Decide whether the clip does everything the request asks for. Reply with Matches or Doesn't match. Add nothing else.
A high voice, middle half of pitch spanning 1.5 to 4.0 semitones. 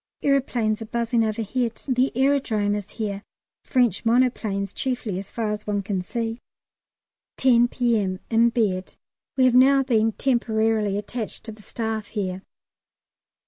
Matches